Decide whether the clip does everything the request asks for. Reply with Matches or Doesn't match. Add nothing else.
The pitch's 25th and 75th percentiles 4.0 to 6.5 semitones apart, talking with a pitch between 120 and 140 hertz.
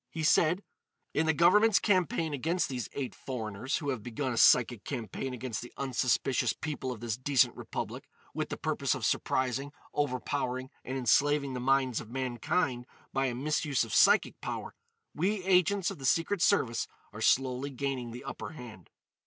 Doesn't match